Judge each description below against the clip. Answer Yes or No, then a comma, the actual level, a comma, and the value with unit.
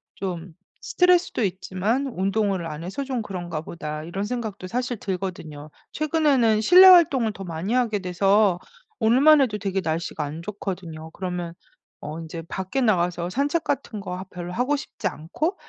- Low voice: No, high, 195 Hz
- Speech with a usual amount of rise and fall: No, wide, 6.1 semitones